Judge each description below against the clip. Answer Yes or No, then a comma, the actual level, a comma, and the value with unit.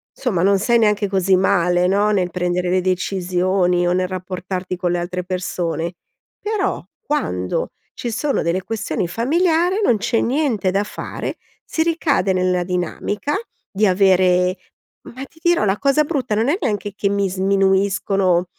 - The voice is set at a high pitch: Yes, high, 195 Hz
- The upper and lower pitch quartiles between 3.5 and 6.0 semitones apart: Yes, average, 4.0 semitones